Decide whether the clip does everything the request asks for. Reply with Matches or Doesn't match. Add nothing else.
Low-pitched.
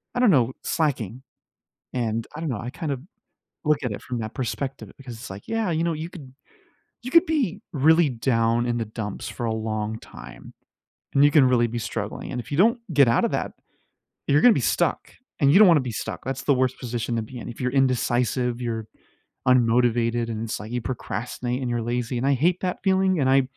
Matches